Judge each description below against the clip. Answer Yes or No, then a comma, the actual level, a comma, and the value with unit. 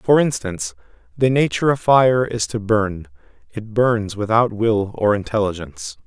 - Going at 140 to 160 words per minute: Yes, average, 150 wpm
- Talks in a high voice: No, low, 115 Hz